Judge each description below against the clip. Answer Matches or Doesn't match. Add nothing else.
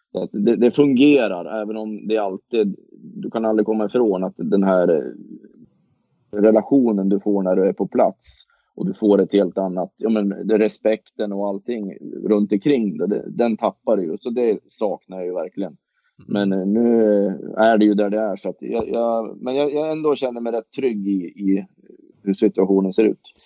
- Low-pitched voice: Matches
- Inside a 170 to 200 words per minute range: Matches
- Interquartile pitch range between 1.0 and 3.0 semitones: Matches